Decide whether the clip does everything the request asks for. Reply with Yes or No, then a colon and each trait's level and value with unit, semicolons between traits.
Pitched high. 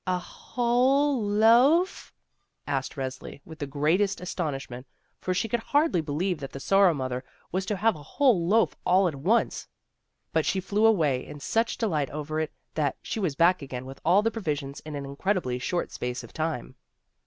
No: medium, 175 Hz